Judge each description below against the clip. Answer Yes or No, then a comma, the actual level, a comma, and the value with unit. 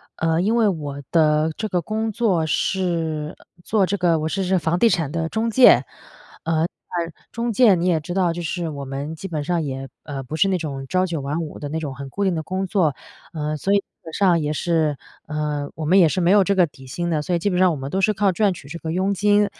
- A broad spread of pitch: No, average, 4.0 semitones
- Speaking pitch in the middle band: Yes, medium, 170 Hz